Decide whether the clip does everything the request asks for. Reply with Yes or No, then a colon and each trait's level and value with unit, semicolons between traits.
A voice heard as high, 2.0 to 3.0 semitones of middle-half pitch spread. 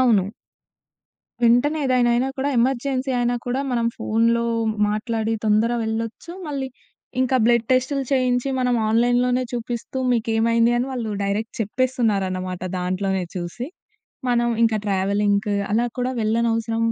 Yes: high, 235 Hz; narrow, 2.6 semitones